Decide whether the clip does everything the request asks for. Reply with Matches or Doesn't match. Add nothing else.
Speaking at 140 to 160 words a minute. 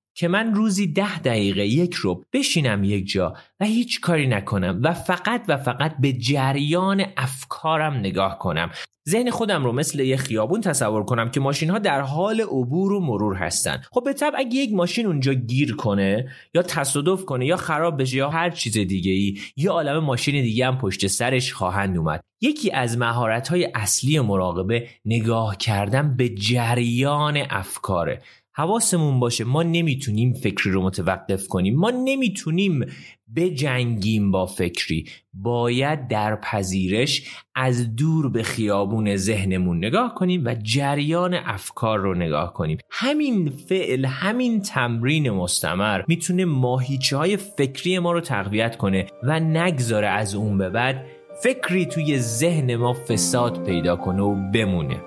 Matches